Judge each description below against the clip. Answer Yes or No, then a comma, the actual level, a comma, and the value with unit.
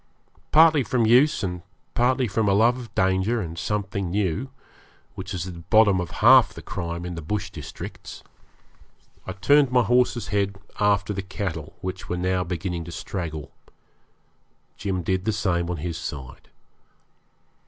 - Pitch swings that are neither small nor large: Yes, average, 3.9 semitones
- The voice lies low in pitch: Yes, very low, 95 Hz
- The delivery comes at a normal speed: Yes, average, 160 wpm